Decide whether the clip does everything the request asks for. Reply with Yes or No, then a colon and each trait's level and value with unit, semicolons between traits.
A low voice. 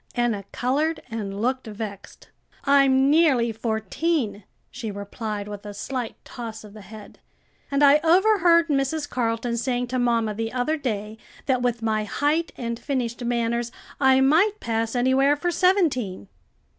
No: high, 245 Hz